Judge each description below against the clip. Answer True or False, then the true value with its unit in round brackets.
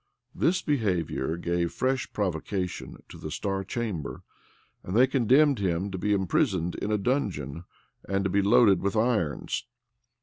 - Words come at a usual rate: True (145 wpm)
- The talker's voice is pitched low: True (100 Hz)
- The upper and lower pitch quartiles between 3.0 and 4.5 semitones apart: False (5.2 semitones)